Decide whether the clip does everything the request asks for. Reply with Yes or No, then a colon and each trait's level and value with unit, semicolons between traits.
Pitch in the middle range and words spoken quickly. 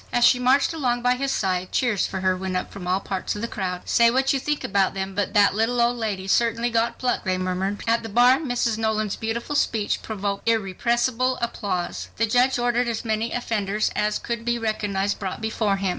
No: high, 220 Hz; fast, 220 wpm